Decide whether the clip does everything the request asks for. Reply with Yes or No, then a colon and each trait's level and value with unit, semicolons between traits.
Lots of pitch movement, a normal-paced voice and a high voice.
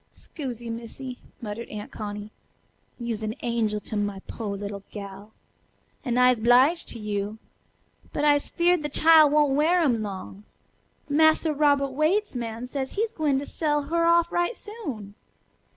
Yes: wide, 6.1 semitones; average, 150 wpm; very high, 255 Hz